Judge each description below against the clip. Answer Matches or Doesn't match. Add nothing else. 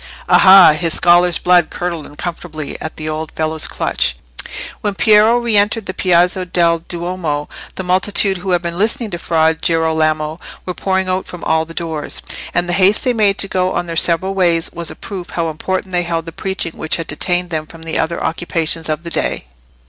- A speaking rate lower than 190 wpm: Doesn't match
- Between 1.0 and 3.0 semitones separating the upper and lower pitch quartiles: Matches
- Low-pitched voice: Doesn't match